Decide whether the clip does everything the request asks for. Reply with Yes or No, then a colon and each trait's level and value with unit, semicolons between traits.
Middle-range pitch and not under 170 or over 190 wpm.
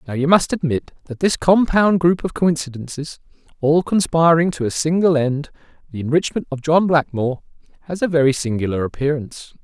No: medium, 155 Hz; average, 150 wpm